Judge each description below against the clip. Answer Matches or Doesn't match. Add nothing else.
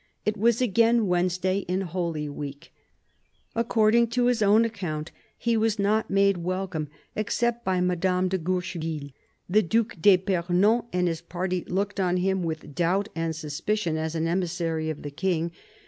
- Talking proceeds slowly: Doesn't match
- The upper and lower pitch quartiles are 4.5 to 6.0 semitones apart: Doesn't match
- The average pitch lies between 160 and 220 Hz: Matches